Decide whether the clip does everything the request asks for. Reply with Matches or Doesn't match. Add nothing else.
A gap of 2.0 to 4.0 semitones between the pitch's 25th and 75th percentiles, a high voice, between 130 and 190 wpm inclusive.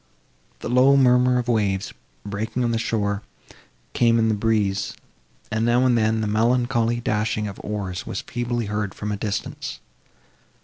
Doesn't match